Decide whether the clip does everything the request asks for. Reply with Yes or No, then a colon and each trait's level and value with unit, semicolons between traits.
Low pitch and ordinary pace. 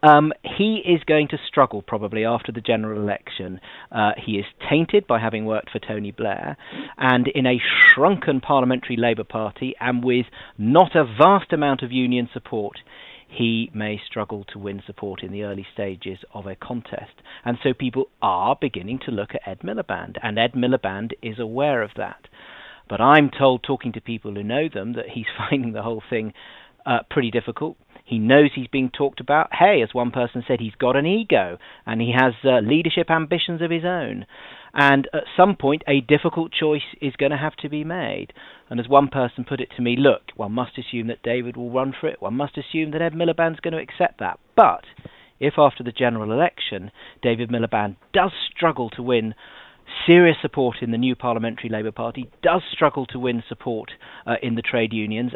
Yes: low, 125 Hz; average, 195 wpm